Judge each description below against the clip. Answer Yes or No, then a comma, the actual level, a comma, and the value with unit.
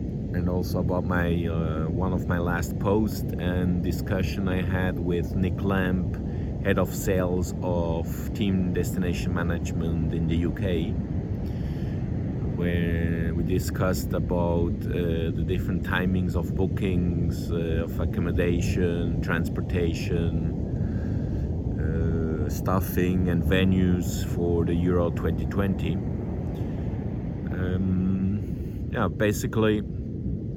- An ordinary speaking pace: No, slow, 105 wpm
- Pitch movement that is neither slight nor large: No, narrow, 2.2 semitones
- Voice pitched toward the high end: No, very low, 90 Hz